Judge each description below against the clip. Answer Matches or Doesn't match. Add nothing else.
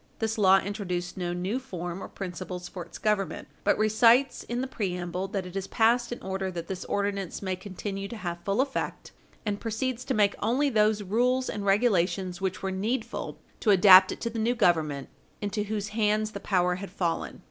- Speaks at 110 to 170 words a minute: Doesn't match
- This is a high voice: Matches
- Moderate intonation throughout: Matches